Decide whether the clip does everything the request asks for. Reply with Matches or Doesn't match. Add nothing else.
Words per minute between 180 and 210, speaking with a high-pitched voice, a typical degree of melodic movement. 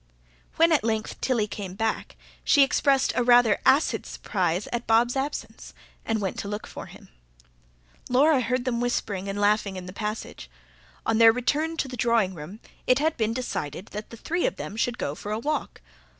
Matches